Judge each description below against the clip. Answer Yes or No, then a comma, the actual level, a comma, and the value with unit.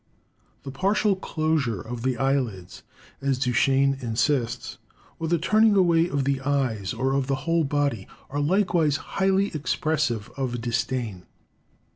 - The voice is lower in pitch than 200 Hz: Yes, medium, 140 Hz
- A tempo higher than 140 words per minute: No, slow, 135 wpm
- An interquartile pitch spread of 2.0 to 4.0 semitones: No, average, 4.6 semitones